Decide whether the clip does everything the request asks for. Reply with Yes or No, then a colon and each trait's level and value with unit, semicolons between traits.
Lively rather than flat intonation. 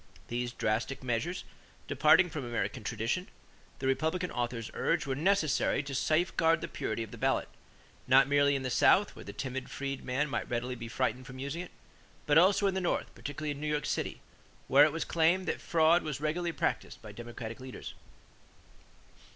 No: average, 4.4 semitones